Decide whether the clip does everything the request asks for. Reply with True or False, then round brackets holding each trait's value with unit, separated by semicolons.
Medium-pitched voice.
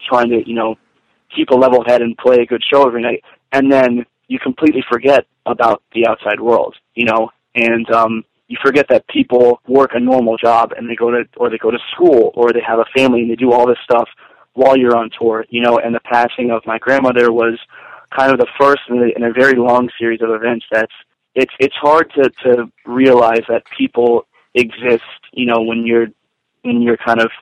False (120 Hz)